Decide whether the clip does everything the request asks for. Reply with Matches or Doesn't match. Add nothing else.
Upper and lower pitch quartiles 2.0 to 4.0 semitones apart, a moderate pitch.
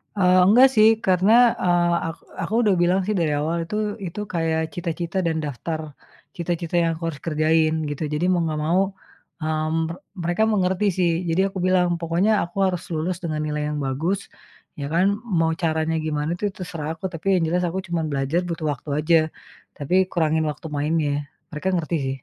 Matches